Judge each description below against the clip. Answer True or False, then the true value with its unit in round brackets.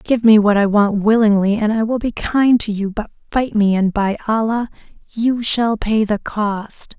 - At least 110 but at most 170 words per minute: False (205 wpm)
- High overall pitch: True (215 Hz)